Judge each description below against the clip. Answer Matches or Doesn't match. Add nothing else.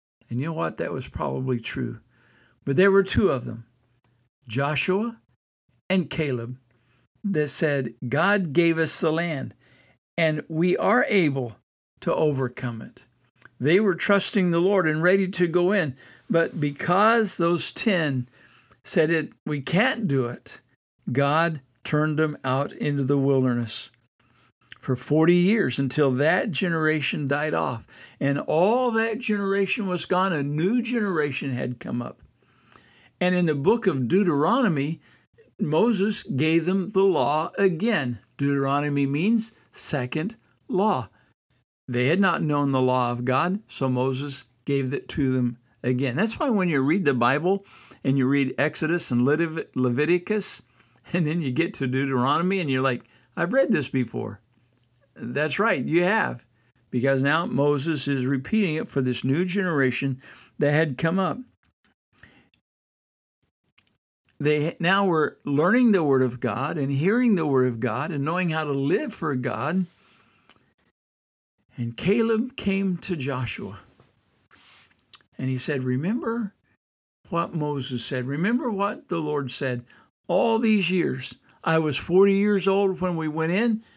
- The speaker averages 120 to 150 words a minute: Matches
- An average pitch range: Doesn't match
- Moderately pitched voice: Matches